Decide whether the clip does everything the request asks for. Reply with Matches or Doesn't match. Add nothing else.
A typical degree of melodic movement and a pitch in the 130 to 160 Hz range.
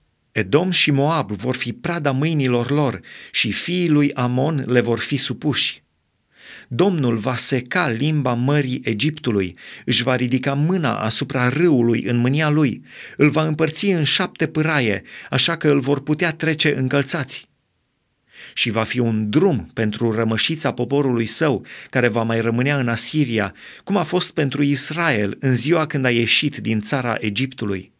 Matches